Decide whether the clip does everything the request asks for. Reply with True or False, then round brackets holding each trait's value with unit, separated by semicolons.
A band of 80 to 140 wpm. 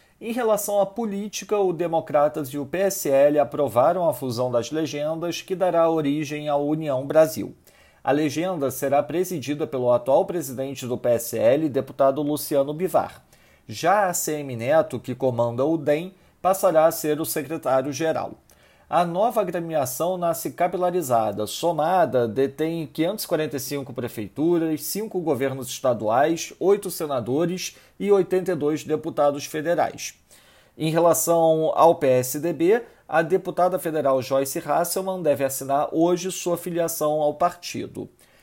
True (125 wpm)